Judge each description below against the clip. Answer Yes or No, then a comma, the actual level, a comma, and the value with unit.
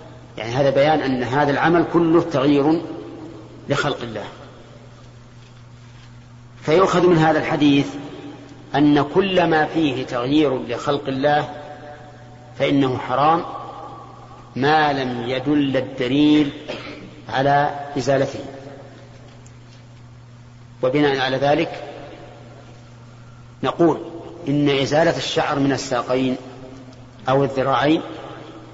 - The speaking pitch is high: No, low, 135 Hz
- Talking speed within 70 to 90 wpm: Yes, average, 85 wpm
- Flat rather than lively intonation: No, average, 3.3 semitones